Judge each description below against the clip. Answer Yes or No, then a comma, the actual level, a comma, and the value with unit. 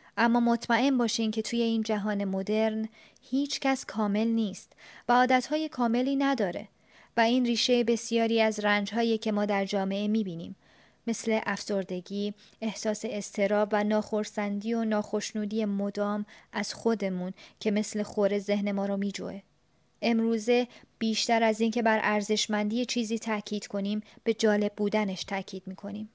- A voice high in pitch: Yes, high, 215 Hz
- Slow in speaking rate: No, average, 135 wpm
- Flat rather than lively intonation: Yes, narrow, 1.9 semitones